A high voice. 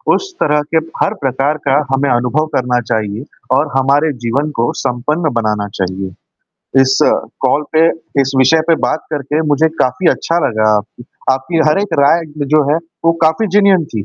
No: medium, 140 Hz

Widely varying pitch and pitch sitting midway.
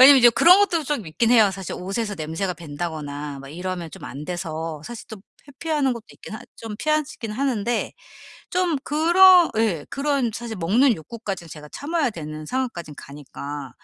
No: wide, 9.0 semitones; high, 215 Hz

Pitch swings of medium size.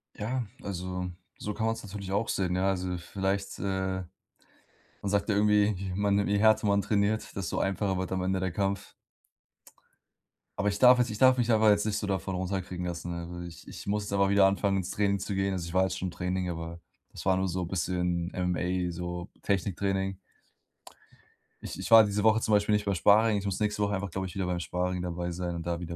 No: narrow, 2.2 semitones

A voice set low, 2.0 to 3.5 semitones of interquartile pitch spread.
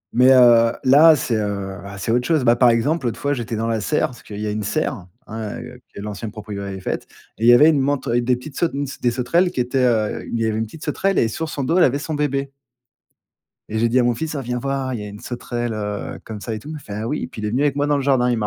No: low, 120 Hz; average, 4.1 semitones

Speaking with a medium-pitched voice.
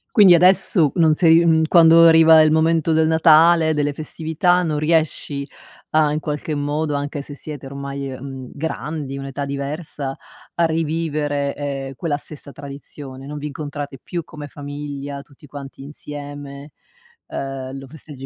Yes: medium, 145 Hz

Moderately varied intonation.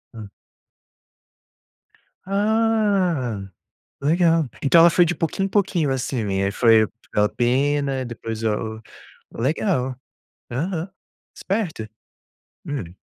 No: wide, 7.8 semitones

